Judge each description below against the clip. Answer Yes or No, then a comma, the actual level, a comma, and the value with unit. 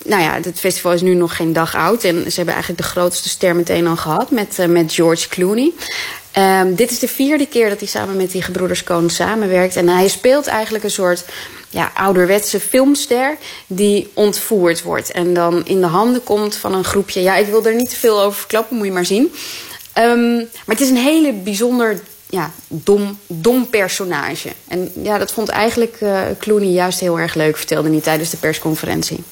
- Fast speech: Yes, fast, 205 wpm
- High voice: Yes, high, 195 Hz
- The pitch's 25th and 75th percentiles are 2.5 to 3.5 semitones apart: No, average, 3.9 semitones